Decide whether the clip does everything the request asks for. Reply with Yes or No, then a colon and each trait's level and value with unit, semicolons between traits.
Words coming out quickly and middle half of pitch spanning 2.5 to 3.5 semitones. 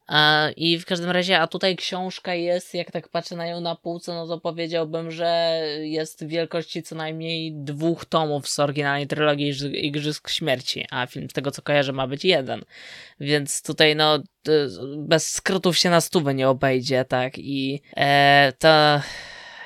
Yes: fast, 165 wpm; average, 2.8 semitones